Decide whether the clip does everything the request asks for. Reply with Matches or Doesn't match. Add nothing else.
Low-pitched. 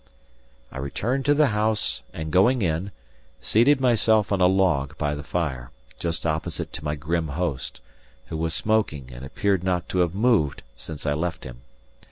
Matches